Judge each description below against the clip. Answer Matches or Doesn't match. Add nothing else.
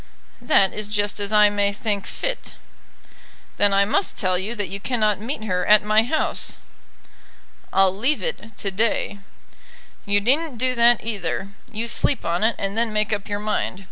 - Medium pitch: Doesn't match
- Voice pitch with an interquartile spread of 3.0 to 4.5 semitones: Doesn't match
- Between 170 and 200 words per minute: Matches